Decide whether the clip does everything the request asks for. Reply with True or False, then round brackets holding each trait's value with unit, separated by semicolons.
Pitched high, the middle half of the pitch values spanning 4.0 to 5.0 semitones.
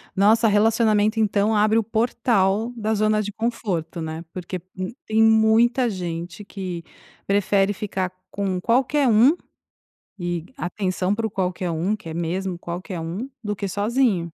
False (205 Hz; 3.4 semitones)